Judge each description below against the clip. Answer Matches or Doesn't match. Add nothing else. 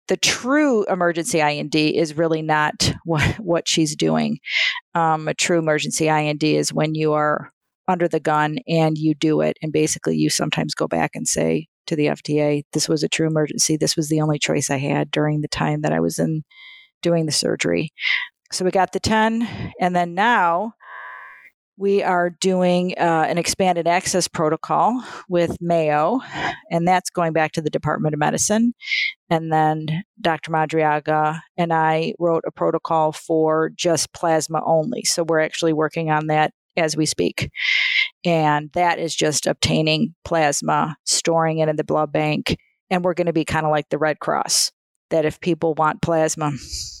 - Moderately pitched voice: Matches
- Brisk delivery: Doesn't match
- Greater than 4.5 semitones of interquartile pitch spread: Doesn't match